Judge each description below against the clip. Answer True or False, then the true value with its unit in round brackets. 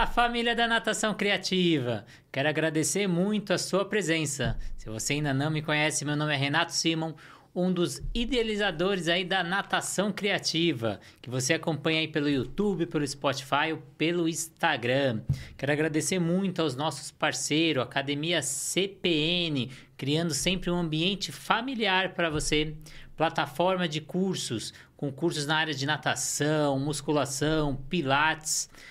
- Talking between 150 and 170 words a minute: False (135 wpm)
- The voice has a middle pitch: True (160 Hz)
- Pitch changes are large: False (3.7 semitones)